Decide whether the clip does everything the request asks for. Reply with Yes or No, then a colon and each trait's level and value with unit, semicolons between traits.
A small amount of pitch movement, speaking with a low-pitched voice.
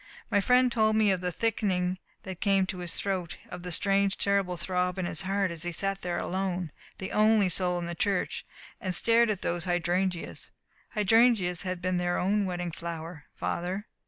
No: narrow, 2.1 semitones; medium, 185 Hz